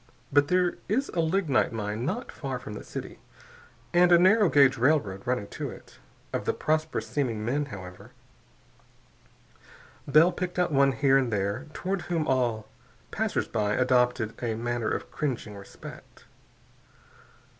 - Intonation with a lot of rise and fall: Yes, wide, 6.2 semitones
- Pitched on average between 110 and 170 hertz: Yes, low, 135 Hz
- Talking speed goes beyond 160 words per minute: No, average, 145 wpm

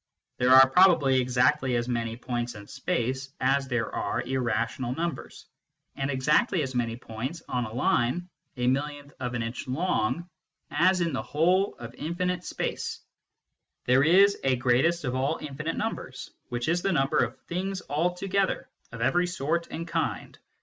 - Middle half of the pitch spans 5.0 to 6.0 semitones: Yes, wide, 5.5 semitones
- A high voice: No, low, 135 Hz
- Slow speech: No, average, 160 wpm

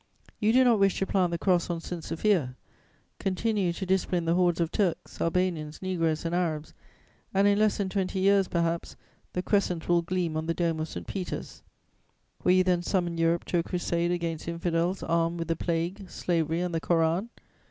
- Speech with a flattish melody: Yes, narrow, 2.1 semitones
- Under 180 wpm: No, average, 195 wpm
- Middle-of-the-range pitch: Yes, medium, 175 Hz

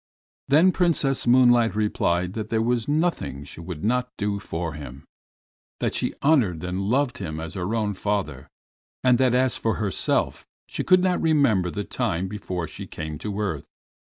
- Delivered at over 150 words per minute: Yes, average, 170 wpm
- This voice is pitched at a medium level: No, low, 105 Hz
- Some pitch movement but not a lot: No, wide, 5.9 semitones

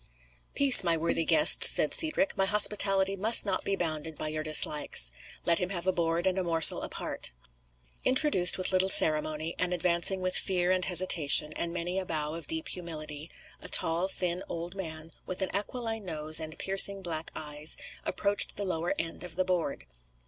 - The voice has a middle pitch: Yes, medium, 175 Hz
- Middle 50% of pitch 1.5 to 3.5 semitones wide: Yes, average, 3.1 semitones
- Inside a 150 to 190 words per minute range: Yes, average, 180 wpm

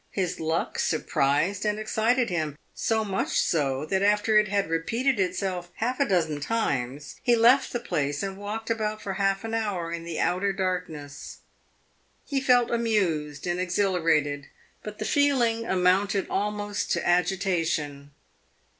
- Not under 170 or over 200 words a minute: No, average, 145 wpm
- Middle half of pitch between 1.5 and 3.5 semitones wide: No, average, 4.8 semitones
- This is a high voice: Yes, high, 195 Hz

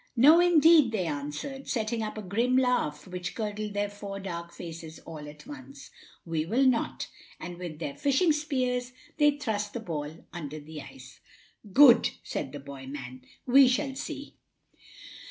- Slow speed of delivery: No, average, 160 wpm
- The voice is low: No, high, 210 Hz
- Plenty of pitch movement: Yes, wide, 8.3 semitones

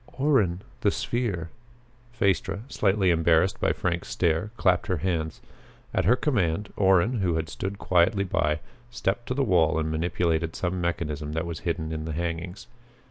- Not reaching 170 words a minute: Yes, average, 160 wpm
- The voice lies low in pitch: Yes, very low, 90 Hz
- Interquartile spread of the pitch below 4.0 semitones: Yes, average, 3.5 semitones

